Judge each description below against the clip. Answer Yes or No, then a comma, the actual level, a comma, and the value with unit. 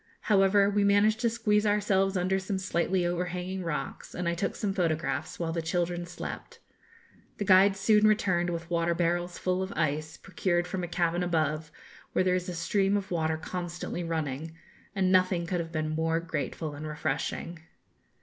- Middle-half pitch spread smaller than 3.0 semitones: Yes, narrow, 2.6 semitones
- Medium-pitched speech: Yes, medium, 175 Hz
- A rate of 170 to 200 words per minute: Yes, average, 175 wpm